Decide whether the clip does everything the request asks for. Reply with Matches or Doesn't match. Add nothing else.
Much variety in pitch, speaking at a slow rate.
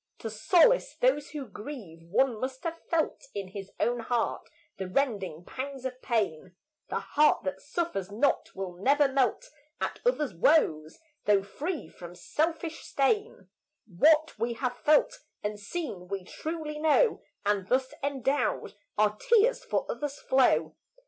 Doesn't match